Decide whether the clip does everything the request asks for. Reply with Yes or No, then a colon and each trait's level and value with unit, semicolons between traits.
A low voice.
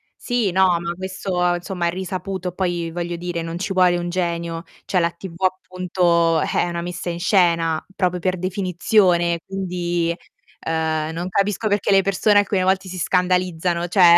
No: medium, 180 Hz